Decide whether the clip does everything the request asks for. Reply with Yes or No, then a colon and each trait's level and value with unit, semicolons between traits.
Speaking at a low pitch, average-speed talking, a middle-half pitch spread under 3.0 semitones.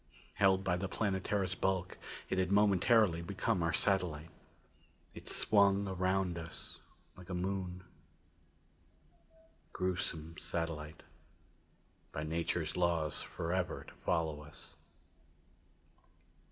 No: very low, 90 Hz; slow, 100 wpm; narrow, 2.6 semitones